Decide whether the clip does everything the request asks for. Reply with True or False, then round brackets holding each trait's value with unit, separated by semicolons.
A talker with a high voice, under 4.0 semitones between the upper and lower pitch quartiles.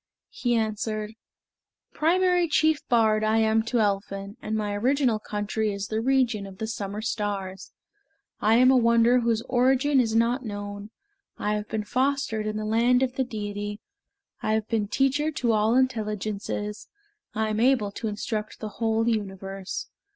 True (220 Hz; 2.9 semitones)